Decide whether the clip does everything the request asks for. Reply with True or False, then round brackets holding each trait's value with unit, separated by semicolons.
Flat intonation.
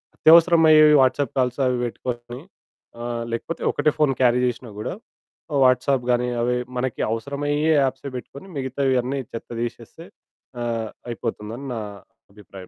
False (3.0 semitones)